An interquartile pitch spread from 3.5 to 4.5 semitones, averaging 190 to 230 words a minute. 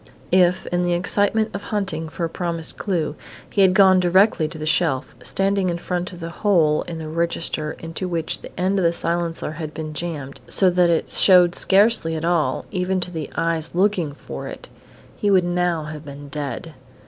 No: average, 2.7 semitones; average, 195 wpm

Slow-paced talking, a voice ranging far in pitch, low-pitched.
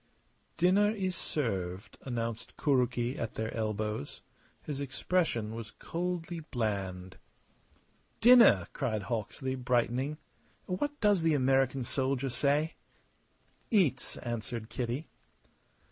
Yes: slow, 100 wpm; wide, 6.0 semitones; low, 130 Hz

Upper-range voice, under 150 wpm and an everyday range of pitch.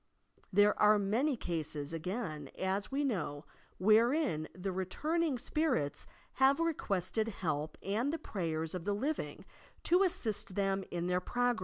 No: high, 200 Hz; average, 140 wpm; wide, 6.8 semitones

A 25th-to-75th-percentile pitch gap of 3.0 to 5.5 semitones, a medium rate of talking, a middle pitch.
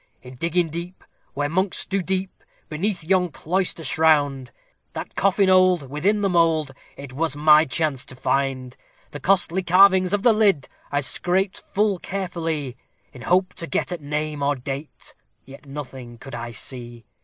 Yes: average, 5.2 semitones; average, 160 wpm; medium, 160 Hz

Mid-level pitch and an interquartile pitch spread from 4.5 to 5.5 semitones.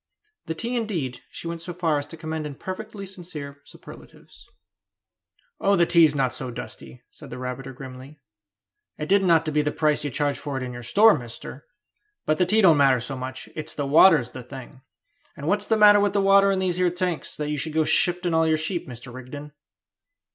Yes: medium, 155 Hz; average, 5.1 semitones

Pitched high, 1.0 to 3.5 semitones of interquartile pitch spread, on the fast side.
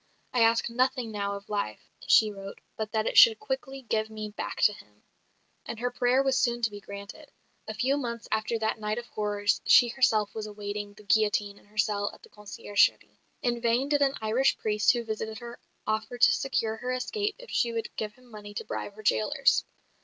Yes: high, 220 Hz; average, 2.8 semitones; fast, 210 wpm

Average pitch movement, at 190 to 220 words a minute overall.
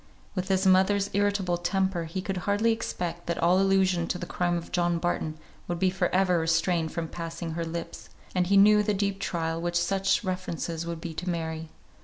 No: narrow, 2.3 semitones; average, 195 wpm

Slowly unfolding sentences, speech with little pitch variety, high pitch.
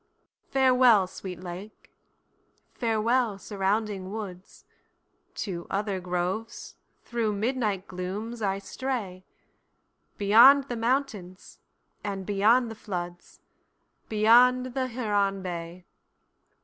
No: slow, 80 wpm; average, 4.0 semitones; high, 210 Hz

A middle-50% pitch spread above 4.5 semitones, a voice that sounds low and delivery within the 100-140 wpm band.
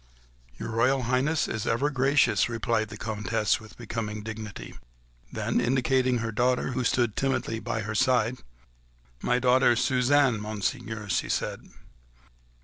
No: average, 2.7 semitones; low, 115 Hz; slow, 135 wpm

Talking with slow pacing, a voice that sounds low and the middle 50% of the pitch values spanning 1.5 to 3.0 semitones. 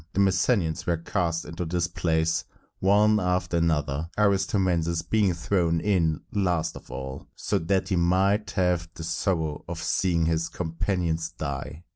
No: average, 145 wpm; very low, 85 Hz; narrow, 2.6 semitones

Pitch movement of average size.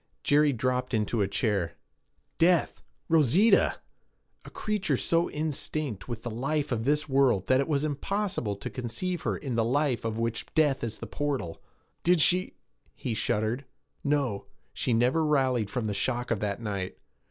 Yes: average, 5.0 semitones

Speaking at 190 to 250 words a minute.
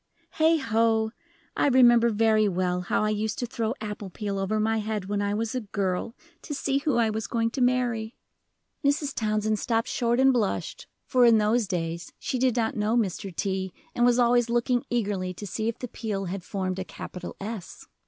Yes: average, 195 wpm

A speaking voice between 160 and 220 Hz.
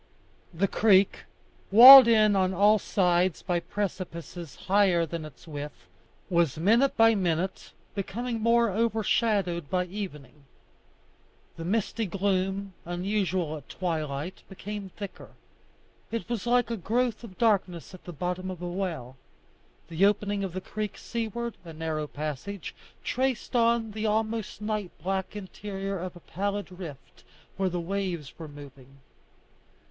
Yes: high, 190 Hz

